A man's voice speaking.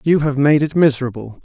Yes: male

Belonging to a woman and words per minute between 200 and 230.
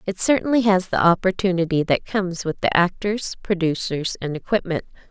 No: female; average, 155 wpm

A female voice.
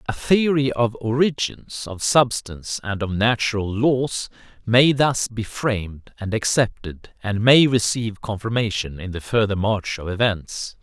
No: male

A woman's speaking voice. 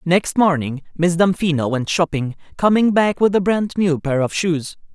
No: male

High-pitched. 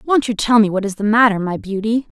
Yes: high, 220 Hz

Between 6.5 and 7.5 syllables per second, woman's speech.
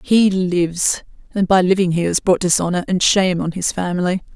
No: 5.4 syllables/s; female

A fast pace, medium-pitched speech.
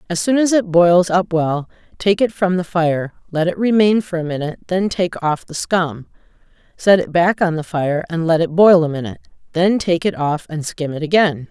Yes: fast, 220 wpm; medium, 175 Hz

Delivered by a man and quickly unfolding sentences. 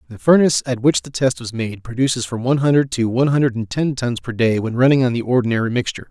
Yes: male; fast, 255 wpm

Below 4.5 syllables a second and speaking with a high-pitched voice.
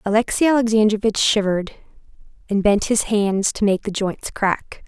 No: 4.9 syllables/s; high, 210 Hz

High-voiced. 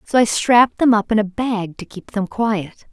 Yes: high, 215 Hz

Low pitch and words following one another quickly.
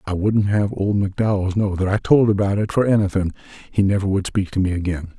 Yes: low, 100 Hz; fast, 220 wpm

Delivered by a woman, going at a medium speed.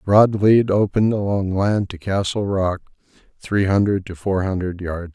No: male; average, 165 wpm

